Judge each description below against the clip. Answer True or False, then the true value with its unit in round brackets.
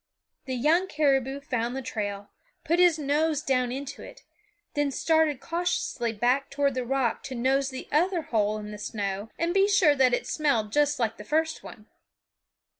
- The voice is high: True (270 Hz)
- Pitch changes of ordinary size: True (4.5 semitones)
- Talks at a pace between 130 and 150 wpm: False (180 wpm)